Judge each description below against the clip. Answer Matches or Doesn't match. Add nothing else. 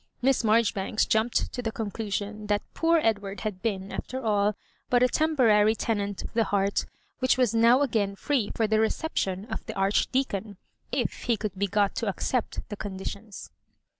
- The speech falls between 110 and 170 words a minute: Doesn't match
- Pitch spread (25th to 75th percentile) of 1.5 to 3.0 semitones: Matches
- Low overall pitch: Doesn't match